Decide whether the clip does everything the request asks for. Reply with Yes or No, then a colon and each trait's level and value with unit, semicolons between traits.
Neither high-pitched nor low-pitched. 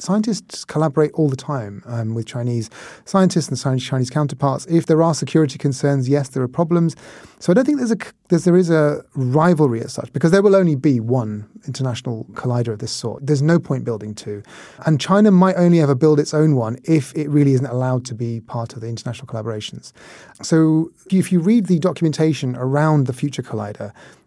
Yes: medium, 145 Hz